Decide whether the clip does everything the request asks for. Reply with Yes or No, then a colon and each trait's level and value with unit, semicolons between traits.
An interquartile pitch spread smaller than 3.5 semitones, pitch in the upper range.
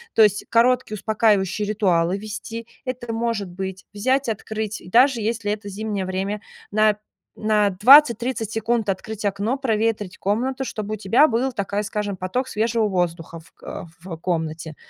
Yes: average, 2.9 semitones; high, 215 Hz